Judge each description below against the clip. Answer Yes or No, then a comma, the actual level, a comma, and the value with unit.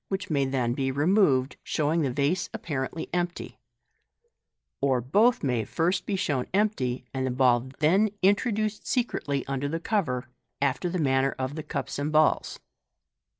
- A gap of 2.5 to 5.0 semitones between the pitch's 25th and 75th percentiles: No, wide, 5.5 semitones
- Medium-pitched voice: Yes, medium, 145 Hz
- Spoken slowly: No, average, 155 wpm